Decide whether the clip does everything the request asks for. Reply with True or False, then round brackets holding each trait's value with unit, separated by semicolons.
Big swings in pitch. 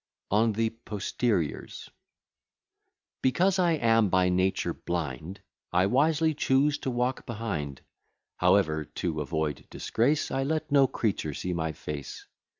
True (7.9 semitones)